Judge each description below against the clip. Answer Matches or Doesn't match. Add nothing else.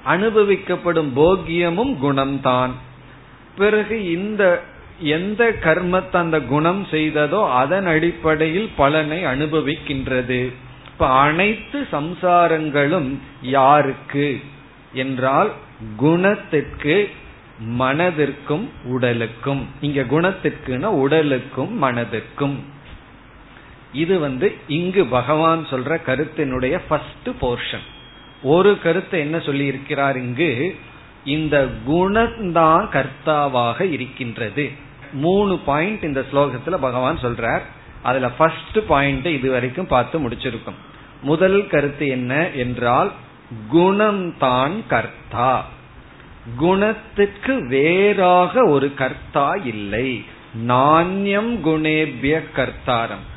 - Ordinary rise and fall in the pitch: Matches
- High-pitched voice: Doesn't match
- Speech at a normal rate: Doesn't match